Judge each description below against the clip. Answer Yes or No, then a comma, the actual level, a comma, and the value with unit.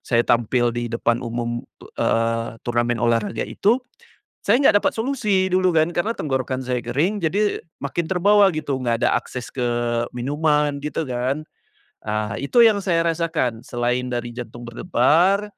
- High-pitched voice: No, low, 130 Hz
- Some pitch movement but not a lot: No, wide, 6.6 semitones